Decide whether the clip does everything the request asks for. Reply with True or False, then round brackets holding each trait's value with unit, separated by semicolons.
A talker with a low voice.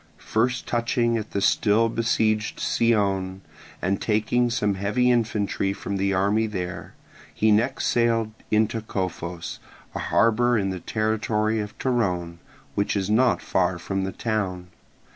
True (105 Hz)